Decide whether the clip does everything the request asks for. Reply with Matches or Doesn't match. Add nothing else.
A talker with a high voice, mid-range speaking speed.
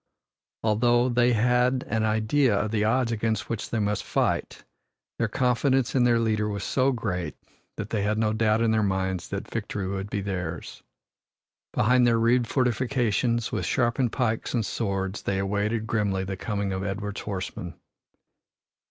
Doesn't match